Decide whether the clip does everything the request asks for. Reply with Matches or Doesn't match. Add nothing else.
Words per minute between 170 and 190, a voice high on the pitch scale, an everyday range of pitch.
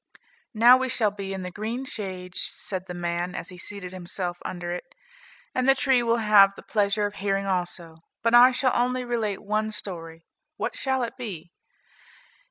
Matches